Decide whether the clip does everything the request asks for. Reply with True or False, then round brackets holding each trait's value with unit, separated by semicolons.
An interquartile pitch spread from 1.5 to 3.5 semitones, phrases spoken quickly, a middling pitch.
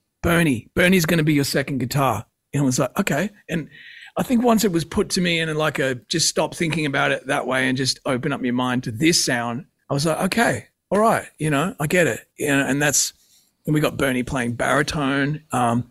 False (4.1 semitones; 240 wpm; 145 Hz)